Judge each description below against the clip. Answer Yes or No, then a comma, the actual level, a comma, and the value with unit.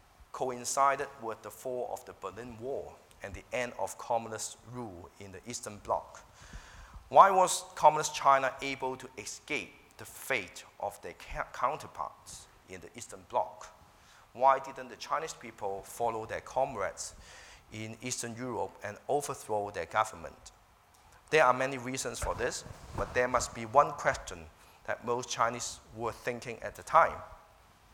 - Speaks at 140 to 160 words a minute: Yes, average, 150 wpm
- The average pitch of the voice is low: Yes, low, 120 Hz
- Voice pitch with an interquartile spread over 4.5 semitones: No, average, 3.0 semitones